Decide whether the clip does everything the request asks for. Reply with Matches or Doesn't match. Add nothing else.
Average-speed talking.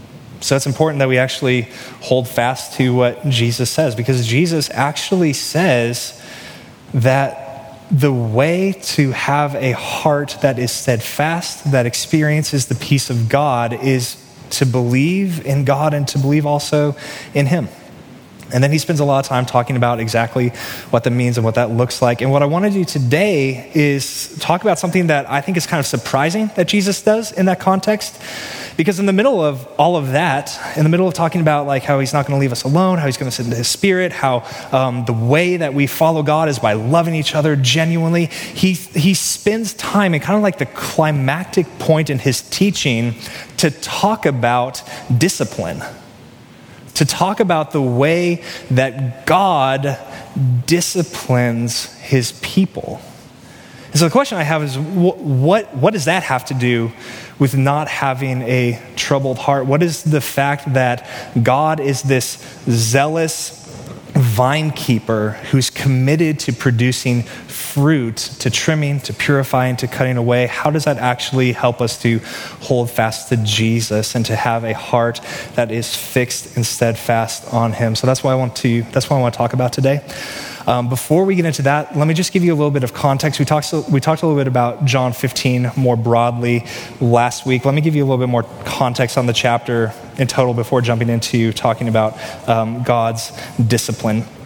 Matches